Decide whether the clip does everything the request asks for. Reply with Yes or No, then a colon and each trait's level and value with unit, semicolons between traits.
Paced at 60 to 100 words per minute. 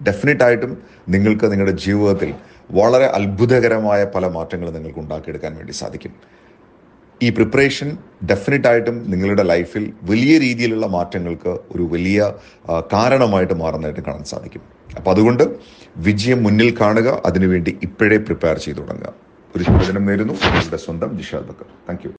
No: average, 120 wpm